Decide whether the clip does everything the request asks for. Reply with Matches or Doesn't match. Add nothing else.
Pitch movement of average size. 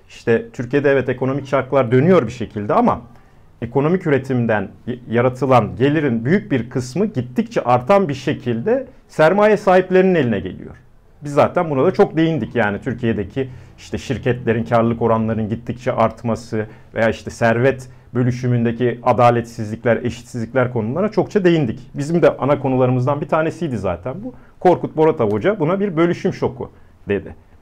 Matches